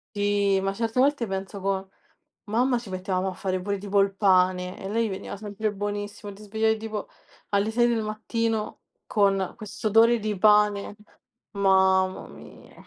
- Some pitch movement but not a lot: No, narrow, 2.2 semitones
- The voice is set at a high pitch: Yes, high, 205 Hz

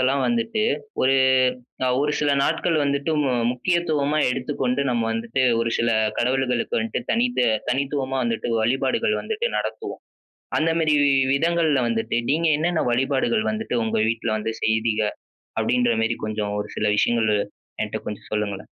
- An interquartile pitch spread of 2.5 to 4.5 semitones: No, average, 5.0 semitones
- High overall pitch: No, low, 130 Hz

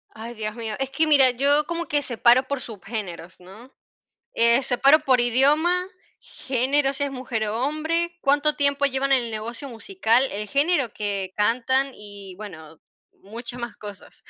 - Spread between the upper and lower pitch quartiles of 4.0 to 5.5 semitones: Yes, average, 4.5 semitones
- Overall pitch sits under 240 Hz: No, very high, 250 Hz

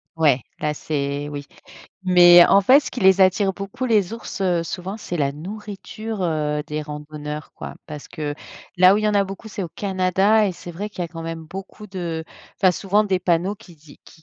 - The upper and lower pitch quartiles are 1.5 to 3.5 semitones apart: No, average, 4.2 semitones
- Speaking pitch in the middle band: Yes, medium, 180 Hz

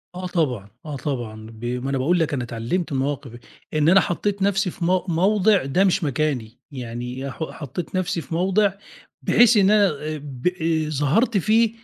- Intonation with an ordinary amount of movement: No, wide, 5.9 semitones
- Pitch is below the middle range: No, medium, 155 Hz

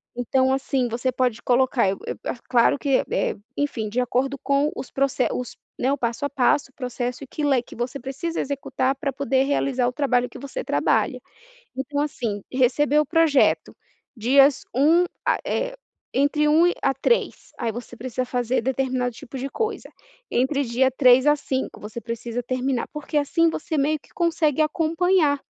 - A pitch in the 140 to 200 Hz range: No, very high, 270 Hz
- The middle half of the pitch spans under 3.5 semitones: Yes, average, 2.7 semitones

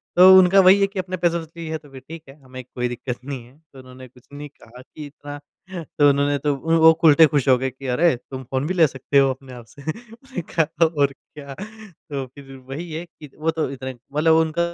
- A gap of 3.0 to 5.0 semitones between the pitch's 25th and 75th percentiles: Yes, average, 4.0 semitones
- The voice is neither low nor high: Yes, medium, 145 Hz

